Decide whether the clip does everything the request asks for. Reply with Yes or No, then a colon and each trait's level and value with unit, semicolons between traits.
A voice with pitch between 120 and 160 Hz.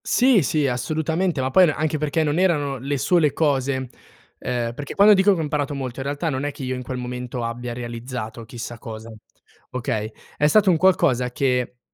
Yes: low, 135 Hz